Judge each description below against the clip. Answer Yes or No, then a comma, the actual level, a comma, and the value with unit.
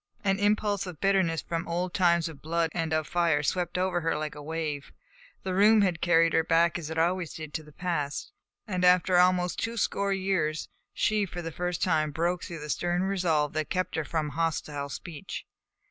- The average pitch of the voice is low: No, medium, 170 Hz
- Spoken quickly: Yes, fast, 210 wpm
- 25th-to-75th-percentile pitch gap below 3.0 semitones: Yes, narrow, 2.5 semitones